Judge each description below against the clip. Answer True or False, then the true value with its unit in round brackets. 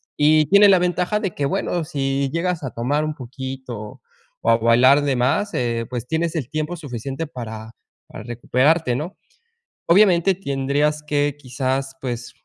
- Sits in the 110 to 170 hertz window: True (140 Hz)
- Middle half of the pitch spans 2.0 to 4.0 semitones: False (4.4 semitones)